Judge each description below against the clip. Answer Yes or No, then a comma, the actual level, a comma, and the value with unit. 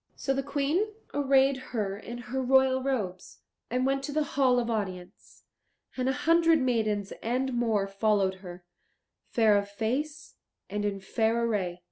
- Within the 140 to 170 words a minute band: Yes, average, 155 wpm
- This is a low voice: No, high, 240 Hz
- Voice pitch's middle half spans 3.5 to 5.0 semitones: Yes, average, 4.7 semitones